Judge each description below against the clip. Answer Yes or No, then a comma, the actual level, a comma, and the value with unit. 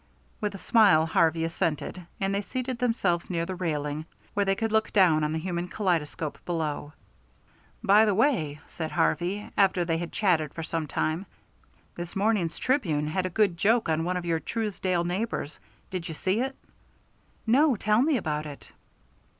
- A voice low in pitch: No, medium, 180 Hz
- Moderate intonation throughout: Yes, average, 4.5 semitones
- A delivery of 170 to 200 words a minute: Yes, average, 175 wpm